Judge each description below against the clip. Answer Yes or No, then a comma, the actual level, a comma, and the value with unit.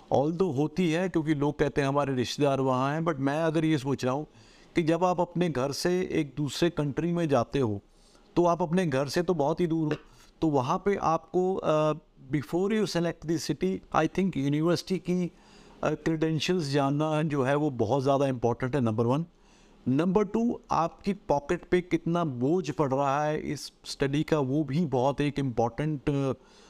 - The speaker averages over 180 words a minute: Yes, fast, 190 wpm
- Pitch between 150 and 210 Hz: Yes, medium, 155 Hz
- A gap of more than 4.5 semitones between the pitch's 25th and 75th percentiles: No, average, 3.9 semitones